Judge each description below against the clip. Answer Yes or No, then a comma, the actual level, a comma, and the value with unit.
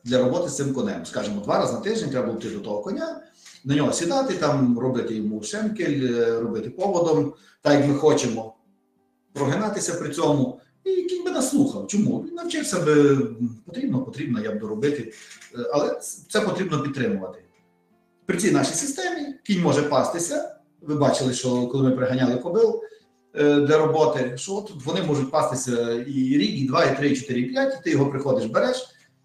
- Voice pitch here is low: No, medium, 150 Hz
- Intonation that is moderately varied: No, wide, 8.7 semitones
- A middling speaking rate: No, fast, 170 wpm